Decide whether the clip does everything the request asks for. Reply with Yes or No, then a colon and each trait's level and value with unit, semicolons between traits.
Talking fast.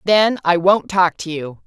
Yes: fast, 215 wpm